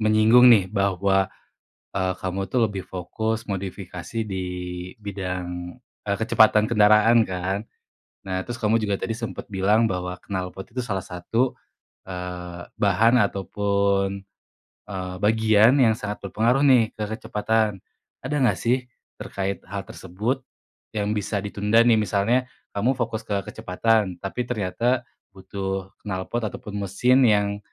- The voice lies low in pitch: Yes, low, 100 Hz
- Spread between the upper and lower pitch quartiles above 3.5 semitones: No, average, 2.9 semitones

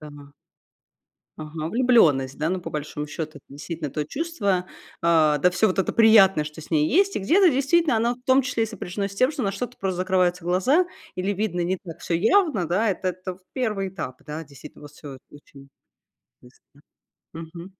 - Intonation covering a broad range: Yes, wide, 6.4 semitones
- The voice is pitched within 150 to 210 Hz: Yes, medium, 185 Hz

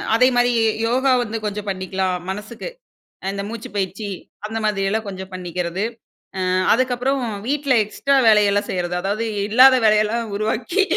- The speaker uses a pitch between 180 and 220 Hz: Yes, high, 215 Hz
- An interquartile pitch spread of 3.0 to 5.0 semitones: Yes, average, 3.8 semitones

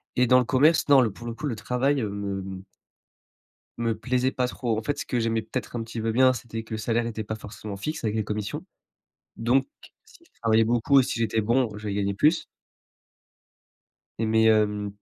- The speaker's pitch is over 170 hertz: No, low, 115 Hz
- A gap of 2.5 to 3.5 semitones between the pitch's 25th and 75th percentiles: Yes, average, 2.8 semitones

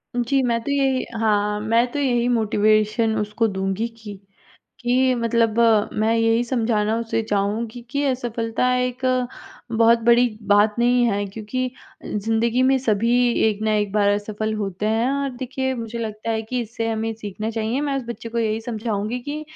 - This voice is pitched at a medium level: No, high, 225 Hz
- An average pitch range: No, narrow, 2.3 semitones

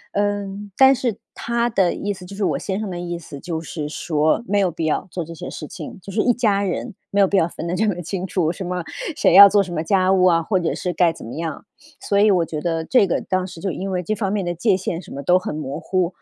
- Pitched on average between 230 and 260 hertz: No, medium, 185 Hz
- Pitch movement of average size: Yes, average, 3.1 semitones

